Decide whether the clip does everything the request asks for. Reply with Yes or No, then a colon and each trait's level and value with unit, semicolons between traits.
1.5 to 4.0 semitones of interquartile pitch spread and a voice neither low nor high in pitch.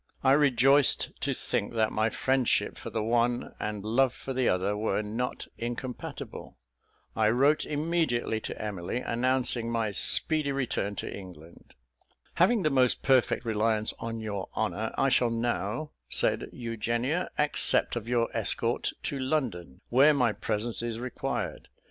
No: average, 3.5 semitones; low, 120 Hz